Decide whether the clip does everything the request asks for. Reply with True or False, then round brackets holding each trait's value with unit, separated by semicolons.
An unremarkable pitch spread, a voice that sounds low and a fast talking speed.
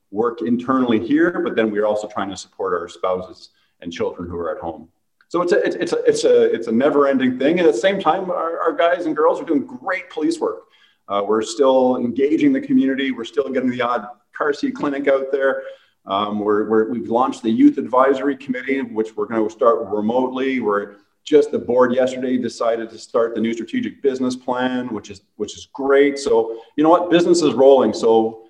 False (7.0 semitones; 130 Hz; 215 wpm)